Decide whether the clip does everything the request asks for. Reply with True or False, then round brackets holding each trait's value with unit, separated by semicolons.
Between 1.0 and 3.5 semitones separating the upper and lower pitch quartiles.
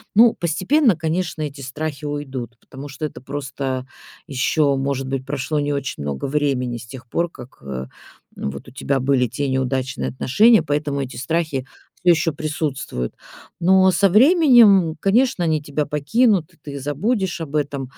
False (4.3 semitones)